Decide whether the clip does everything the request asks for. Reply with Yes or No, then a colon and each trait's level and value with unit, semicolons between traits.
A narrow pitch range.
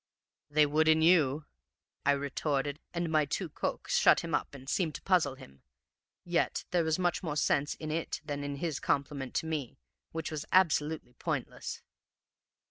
Yes: narrow, 2.3 semitones